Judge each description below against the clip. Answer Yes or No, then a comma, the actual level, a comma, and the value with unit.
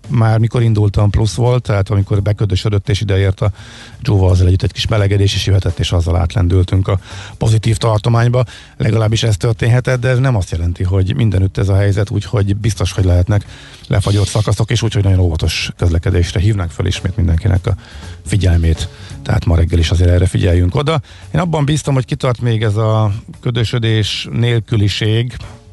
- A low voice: Yes, low, 105 Hz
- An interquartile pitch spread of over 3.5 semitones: No, average, 3.2 semitones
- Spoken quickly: Yes, fast, 170 wpm